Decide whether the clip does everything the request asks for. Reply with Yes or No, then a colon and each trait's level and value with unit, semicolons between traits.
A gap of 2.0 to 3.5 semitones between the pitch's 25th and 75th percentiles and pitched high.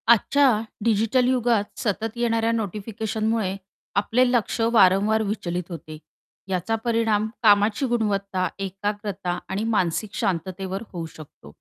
Yes: average, 2.9 semitones; high, 210 Hz